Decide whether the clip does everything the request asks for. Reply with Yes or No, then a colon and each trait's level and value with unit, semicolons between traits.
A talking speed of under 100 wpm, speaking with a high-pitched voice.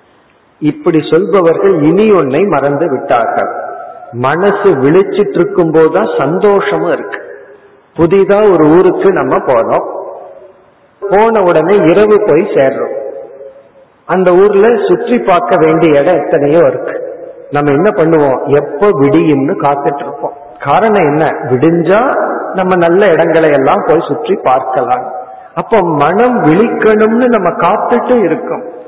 No: average, 105 wpm; high, 195 Hz